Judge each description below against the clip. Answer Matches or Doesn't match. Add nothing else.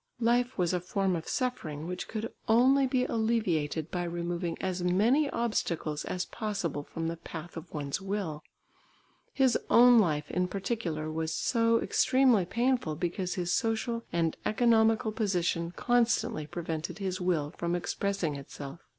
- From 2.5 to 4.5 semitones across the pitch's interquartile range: Doesn't match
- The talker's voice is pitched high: Doesn't match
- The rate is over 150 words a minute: Doesn't match